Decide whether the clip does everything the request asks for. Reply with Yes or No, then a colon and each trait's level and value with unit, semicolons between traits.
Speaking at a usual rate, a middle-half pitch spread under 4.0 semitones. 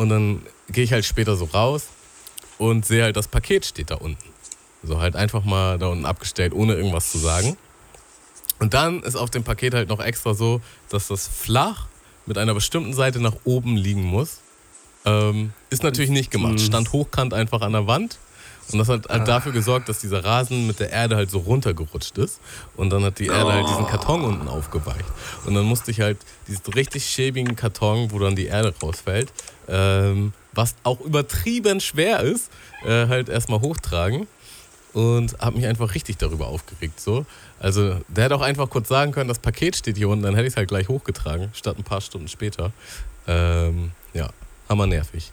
No: fast, 195 wpm; average, 3.5 semitones